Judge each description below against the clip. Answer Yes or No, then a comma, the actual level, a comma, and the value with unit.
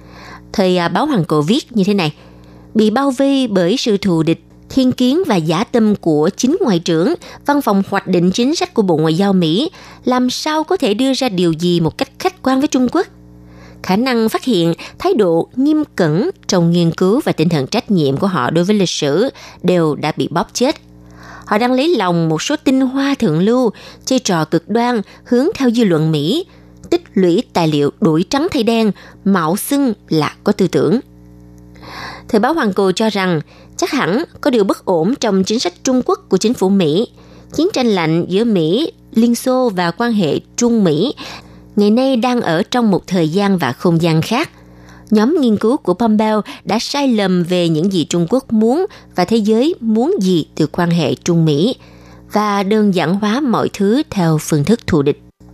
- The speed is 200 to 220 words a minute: Yes, average, 205 wpm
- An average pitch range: No, wide, 6.8 semitones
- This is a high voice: Yes, high, 195 Hz